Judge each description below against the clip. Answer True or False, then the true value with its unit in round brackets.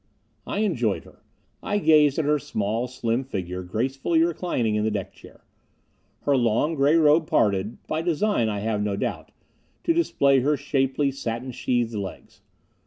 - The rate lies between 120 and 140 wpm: False (160 wpm)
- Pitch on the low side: True (130 Hz)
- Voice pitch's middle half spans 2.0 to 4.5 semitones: False (5.6 semitones)